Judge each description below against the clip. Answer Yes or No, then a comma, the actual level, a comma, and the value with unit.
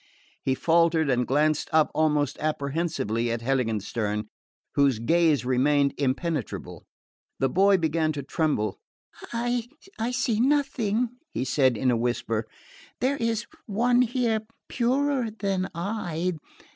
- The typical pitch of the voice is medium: Yes, medium, 160 Hz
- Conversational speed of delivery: No, slow, 120 wpm